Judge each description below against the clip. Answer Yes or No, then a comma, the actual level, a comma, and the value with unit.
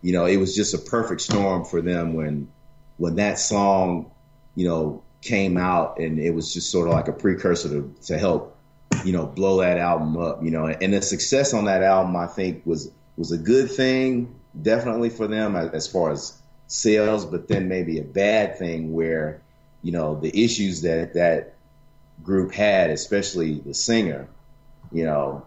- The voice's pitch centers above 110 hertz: No, very low, 90 Hz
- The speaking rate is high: No, average, 185 wpm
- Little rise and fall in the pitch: No, average, 3.8 semitones